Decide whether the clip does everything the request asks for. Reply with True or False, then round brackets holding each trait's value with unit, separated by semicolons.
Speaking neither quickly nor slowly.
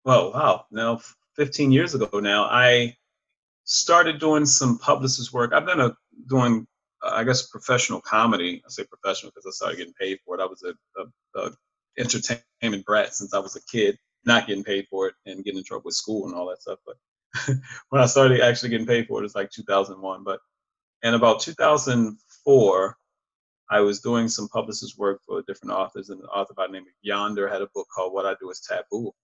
False (210 wpm)